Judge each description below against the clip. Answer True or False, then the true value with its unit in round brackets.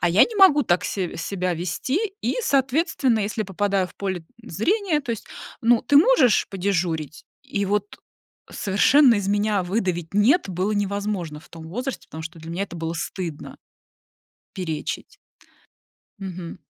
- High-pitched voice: True (200 Hz)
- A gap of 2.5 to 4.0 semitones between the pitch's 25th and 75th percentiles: False (5.0 semitones)